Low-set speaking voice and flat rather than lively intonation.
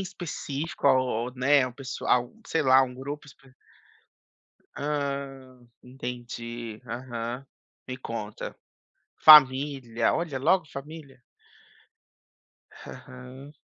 Yes: low, 130 Hz; narrow, 2.3 semitones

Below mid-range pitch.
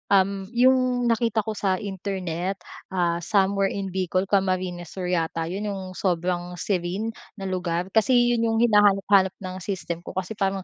No: high, 190 Hz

